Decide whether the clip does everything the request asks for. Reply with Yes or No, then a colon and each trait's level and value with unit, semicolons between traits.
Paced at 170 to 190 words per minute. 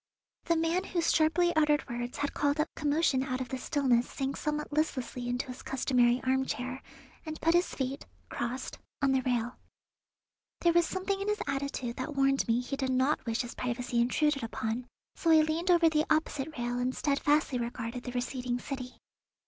Yes: average, 180 wpm